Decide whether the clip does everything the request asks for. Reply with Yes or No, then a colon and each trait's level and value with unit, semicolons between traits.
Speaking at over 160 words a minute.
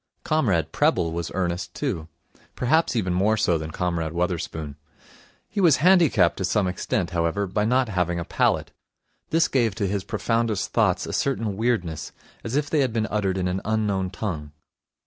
Yes: average, 170 wpm